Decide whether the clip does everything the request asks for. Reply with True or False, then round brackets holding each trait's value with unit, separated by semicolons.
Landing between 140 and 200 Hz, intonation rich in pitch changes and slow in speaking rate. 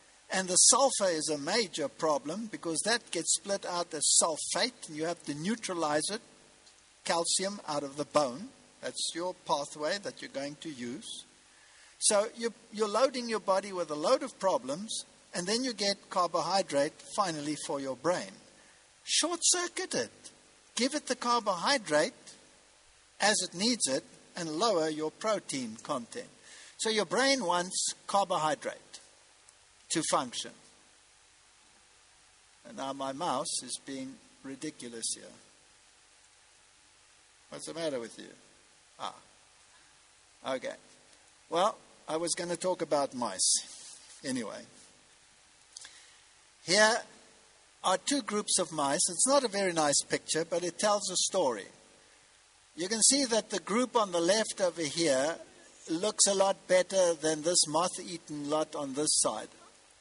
True (185 Hz; 6.3 semitones; 140 wpm)